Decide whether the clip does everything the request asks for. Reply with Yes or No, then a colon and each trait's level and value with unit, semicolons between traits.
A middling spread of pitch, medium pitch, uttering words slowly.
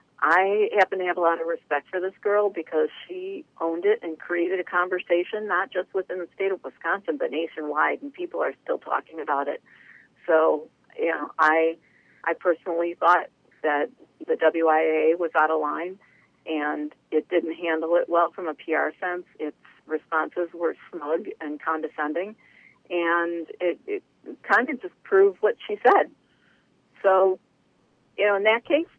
No: average, 3.5 semitones; medium, 175 Hz; average, 170 wpm